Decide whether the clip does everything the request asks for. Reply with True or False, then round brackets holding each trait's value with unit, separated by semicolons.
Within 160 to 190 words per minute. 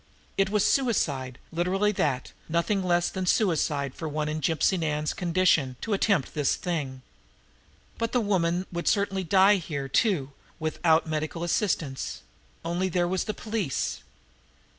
False (145 wpm)